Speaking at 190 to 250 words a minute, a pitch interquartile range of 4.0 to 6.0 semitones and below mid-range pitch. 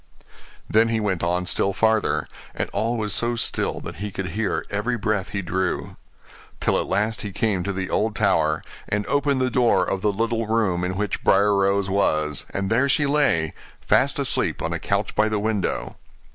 No: average, 195 wpm; average, 3.0 semitones; low, 105 Hz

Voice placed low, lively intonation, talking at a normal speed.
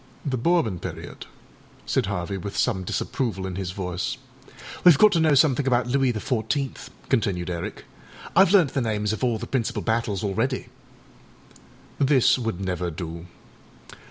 Yes: low, 110 Hz; wide, 6.1 semitones; average, 155 wpm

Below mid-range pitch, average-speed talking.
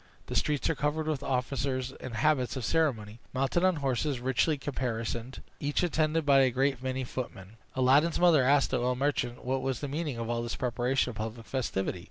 Yes: low, 130 Hz; average, 195 wpm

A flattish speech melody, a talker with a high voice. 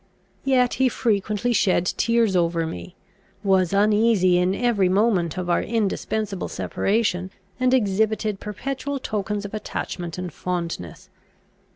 No: average, 3.9 semitones; high, 205 Hz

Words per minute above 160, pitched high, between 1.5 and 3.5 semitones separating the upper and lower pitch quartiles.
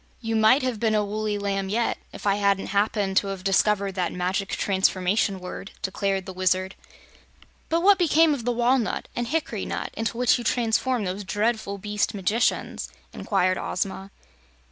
Yes: average, 170 wpm; high, 205 Hz; average, 3.2 semitones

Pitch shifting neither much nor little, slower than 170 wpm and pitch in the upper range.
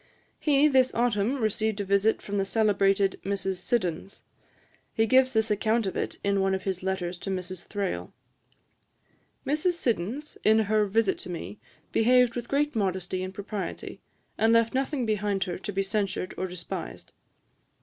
Yes: average, 3.3 semitones; average, 160 wpm; high, 205 Hz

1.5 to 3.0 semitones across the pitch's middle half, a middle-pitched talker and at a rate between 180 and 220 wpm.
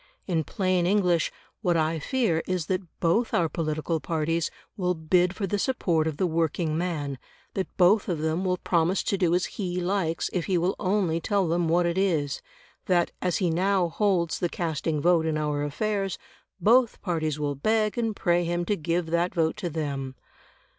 Yes: average, 2.7 semitones; medium, 175 Hz; average, 190 wpm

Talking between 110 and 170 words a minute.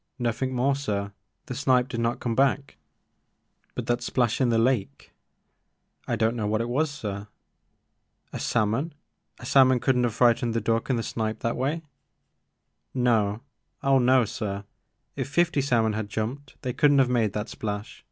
No: average, 195 wpm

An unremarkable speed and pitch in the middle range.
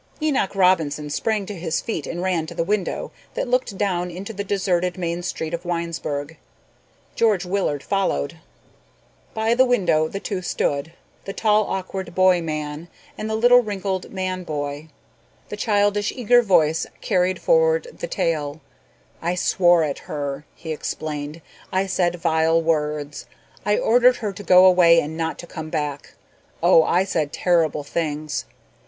Yes: average, 155 wpm; medium, 175 Hz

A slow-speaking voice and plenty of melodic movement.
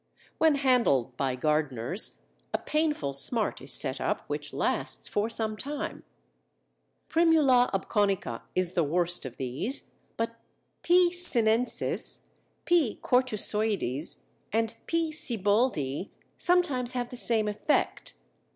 Yes: slow, 115 wpm; wide, 7.3 semitones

